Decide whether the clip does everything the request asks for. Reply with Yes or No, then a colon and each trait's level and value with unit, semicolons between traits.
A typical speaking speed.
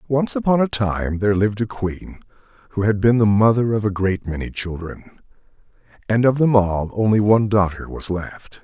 Yes: average, 190 wpm